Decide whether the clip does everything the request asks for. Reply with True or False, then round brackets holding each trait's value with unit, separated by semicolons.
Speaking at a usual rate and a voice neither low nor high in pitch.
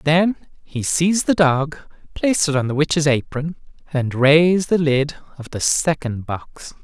True (165 wpm; 150 Hz)